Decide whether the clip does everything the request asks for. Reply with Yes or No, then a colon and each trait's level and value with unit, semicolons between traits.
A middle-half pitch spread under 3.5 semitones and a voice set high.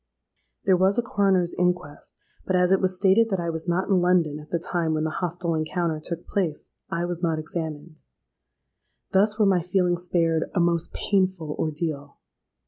No: narrow, 2.6 semitones; medium, 175 Hz